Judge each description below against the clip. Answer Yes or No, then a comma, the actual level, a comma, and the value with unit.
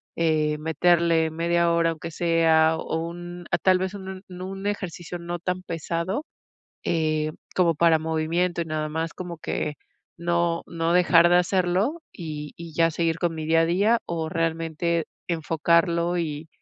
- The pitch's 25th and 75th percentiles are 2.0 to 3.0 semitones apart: No, narrow, 1.5 semitones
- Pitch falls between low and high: Yes, medium, 170 Hz